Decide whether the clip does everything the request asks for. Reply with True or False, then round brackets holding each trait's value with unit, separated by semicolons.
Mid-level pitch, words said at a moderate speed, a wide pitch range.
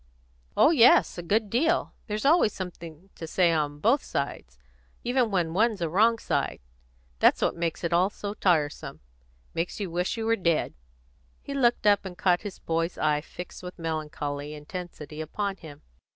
False (180 Hz; 170 wpm; 4.7 semitones)